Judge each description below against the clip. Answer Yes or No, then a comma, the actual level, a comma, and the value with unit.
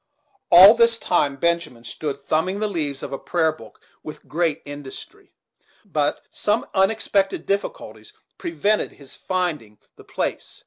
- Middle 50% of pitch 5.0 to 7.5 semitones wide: Yes, wide, 5.6 semitones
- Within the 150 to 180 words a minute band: No, slow, 135 wpm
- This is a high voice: No, medium, 170 Hz